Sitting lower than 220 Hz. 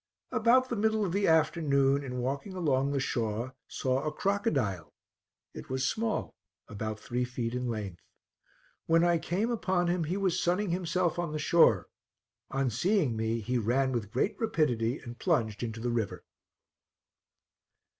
Yes: medium, 140 Hz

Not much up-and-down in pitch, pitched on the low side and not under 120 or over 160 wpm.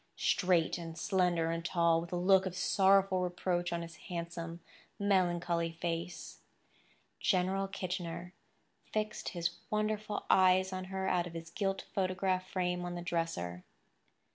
No: narrow, 1.9 semitones; medium, 180 Hz; average, 140 wpm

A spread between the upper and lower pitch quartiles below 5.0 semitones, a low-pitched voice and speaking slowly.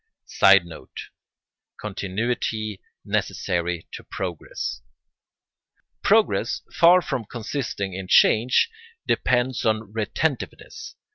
Yes: average, 4.5 semitones; low, 110 Hz; slow, 75 wpm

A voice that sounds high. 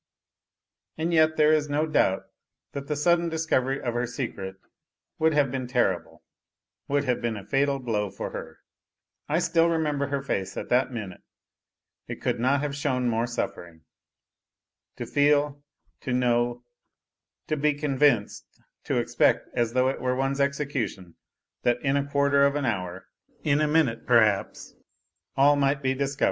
No: low, 135 Hz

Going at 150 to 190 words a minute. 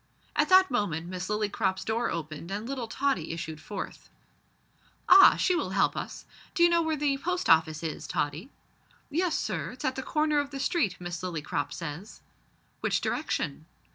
Yes: average, 170 wpm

